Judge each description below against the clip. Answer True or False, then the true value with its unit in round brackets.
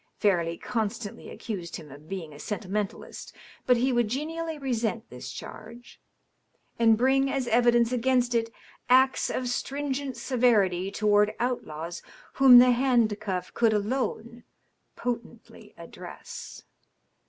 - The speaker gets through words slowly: True (130 wpm)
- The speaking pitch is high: True (235 Hz)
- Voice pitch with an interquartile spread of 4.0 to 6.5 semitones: False (3.5 semitones)